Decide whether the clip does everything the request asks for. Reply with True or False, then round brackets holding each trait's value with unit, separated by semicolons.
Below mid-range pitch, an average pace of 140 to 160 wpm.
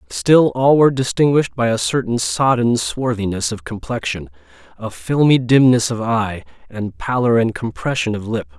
True (120 Hz; 155 wpm)